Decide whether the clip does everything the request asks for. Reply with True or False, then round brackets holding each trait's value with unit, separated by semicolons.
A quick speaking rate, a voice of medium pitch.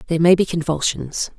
False (175 wpm; 165 Hz)